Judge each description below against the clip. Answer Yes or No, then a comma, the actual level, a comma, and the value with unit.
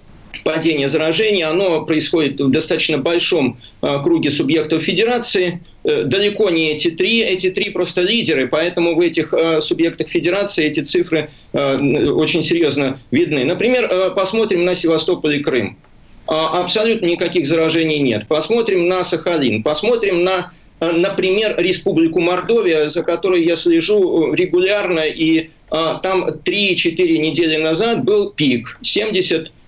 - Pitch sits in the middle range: Yes, medium, 175 Hz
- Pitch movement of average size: Yes, average, 3.4 semitones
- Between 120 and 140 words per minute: Yes, average, 135 wpm